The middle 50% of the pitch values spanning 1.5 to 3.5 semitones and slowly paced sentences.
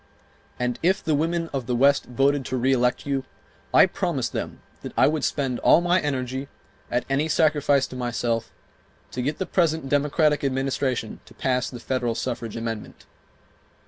No: average, 3.1 semitones; average, 165 wpm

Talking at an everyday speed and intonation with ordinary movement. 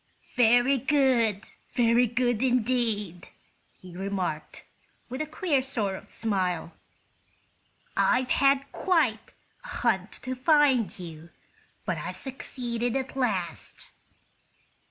No: slow, 105 wpm; average, 4.7 semitones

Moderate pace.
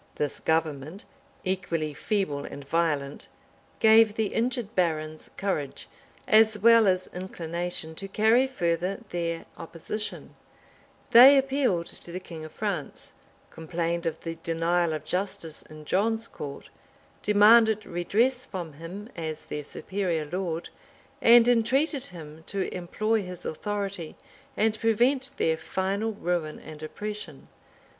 No: slow, 125 wpm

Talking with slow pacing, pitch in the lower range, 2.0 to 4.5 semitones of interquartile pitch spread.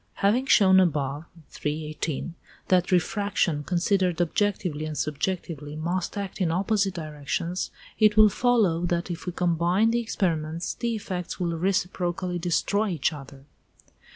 No: slow, 130 wpm; medium, 175 Hz; average, 3.6 semitones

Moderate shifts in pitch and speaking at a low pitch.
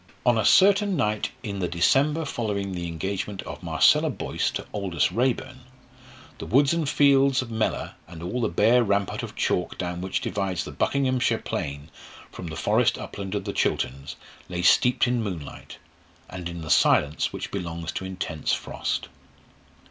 No: wide, 6.3 semitones; low, 100 Hz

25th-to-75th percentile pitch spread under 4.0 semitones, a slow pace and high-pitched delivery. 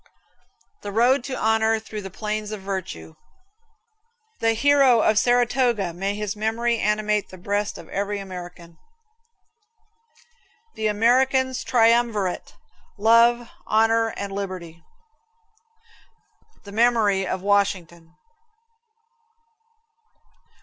Yes: average, 3.0 semitones; slow, 95 wpm; high, 210 Hz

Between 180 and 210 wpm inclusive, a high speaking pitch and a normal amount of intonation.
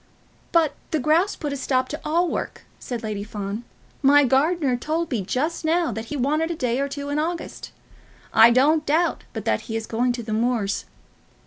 Yes: average, 200 wpm; very high, 280 Hz; average, 5.0 semitones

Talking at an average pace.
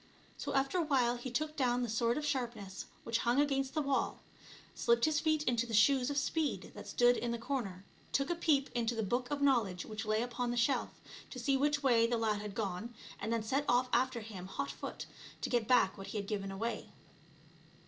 No: fast, 220 wpm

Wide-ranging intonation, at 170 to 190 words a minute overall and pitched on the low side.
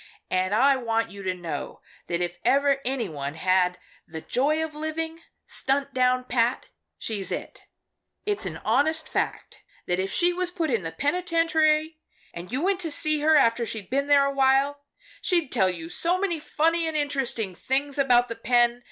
No: wide, 6.3 semitones; average, 180 wpm; very high, 270 Hz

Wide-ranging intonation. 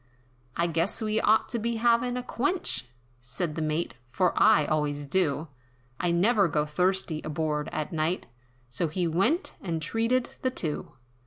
Yes: wide, 6.4 semitones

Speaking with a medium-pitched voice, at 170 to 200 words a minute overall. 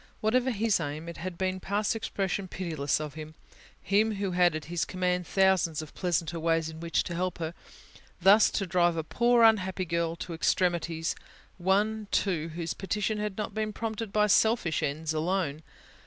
Yes: medium, 180 Hz; average, 175 wpm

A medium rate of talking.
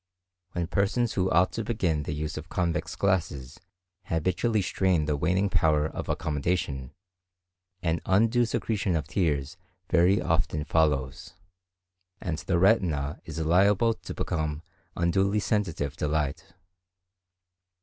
No: slow, 125 wpm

